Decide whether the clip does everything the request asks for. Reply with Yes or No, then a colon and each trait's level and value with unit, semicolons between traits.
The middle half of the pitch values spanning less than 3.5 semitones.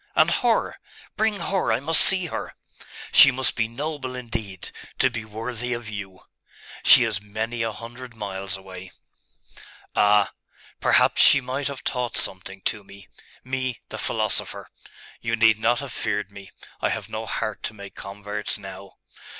No: average, 4.0 semitones